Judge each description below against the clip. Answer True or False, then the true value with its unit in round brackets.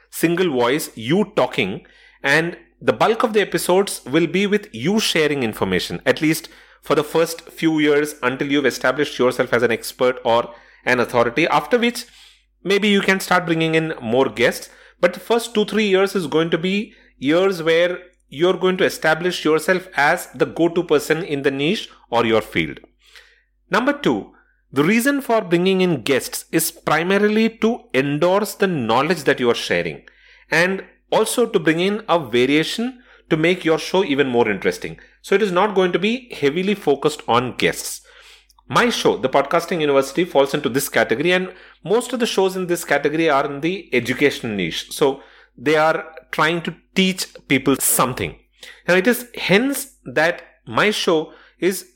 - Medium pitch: True (170 Hz)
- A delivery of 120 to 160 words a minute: False (175 wpm)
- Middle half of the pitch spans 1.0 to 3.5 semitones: False (5.2 semitones)